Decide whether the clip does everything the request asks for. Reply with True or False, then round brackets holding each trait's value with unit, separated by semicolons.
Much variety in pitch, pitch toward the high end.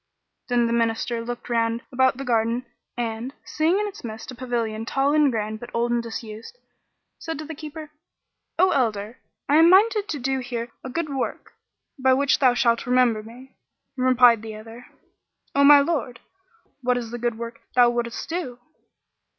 False (3.2 semitones; 245 Hz)